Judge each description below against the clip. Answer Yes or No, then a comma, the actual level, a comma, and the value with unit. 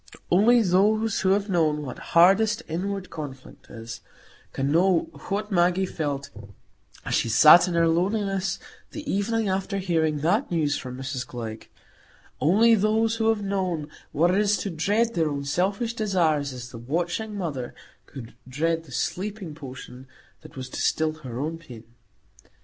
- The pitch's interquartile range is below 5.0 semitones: No, wide, 5.6 semitones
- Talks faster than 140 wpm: Yes, average, 155 wpm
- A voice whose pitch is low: No, medium, 175 Hz